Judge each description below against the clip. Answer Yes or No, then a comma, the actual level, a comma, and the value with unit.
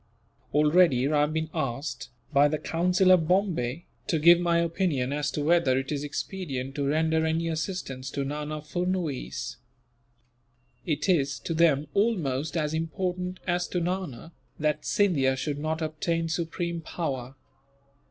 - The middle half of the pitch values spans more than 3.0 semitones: Yes, average, 3.4 semitones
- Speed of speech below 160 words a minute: Yes, average, 145 wpm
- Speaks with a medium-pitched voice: Yes, medium, 160 Hz